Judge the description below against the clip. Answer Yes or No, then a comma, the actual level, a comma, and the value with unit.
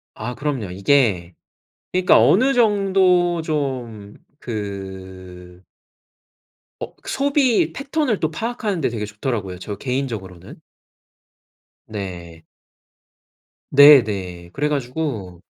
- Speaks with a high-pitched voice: No, low, 125 Hz